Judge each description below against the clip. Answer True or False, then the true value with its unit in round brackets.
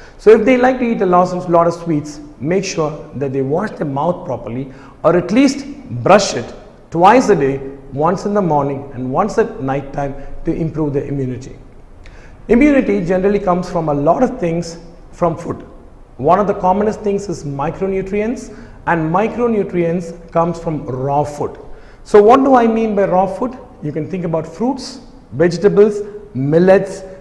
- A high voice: False (175 Hz)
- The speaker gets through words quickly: True (170 wpm)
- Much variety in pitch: True (5.7 semitones)